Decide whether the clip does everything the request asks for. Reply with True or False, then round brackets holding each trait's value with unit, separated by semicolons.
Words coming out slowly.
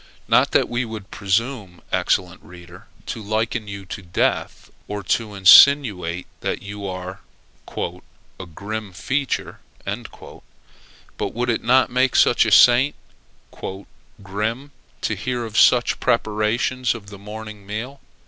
True (125 wpm)